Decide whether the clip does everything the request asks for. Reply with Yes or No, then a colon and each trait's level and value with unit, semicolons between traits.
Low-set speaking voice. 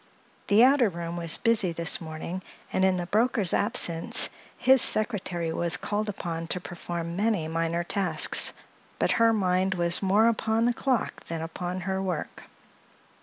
No: medium, 185 Hz